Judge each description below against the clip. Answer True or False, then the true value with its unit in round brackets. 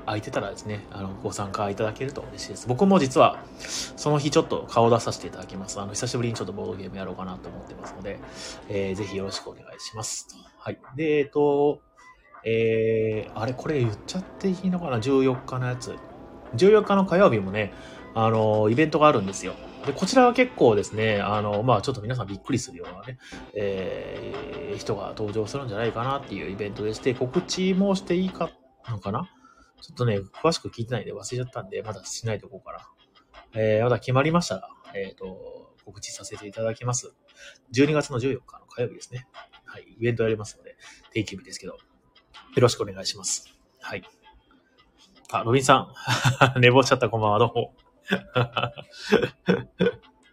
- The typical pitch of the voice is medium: False (120 Hz)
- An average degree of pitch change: True (4.9 semitones)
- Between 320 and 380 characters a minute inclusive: False (390 characters per minute)